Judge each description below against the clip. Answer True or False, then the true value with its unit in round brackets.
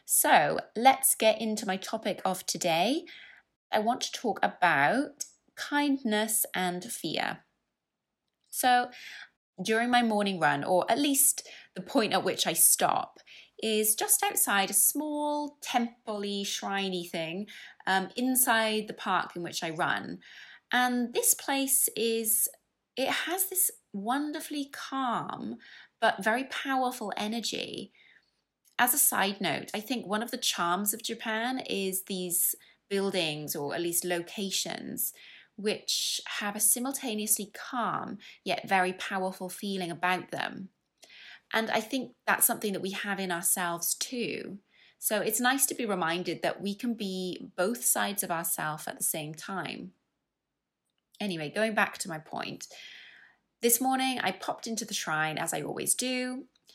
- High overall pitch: True (215 Hz)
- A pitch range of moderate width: True (5.0 semitones)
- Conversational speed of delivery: True (145 wpm)